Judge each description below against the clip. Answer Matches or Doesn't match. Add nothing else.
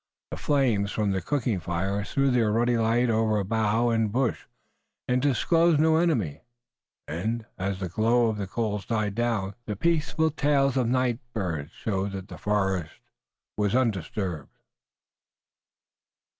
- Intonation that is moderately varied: Matches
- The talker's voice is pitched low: Matches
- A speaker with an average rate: Matches